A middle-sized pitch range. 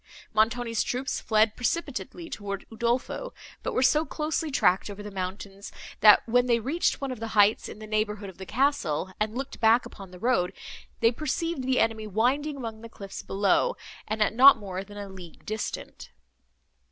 Yes: average, 4.1 semitones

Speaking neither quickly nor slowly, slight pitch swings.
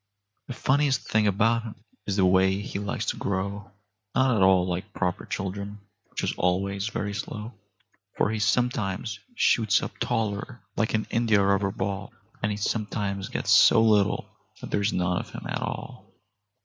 Yes: average, 170 wpm; narrow, 2.2 semitones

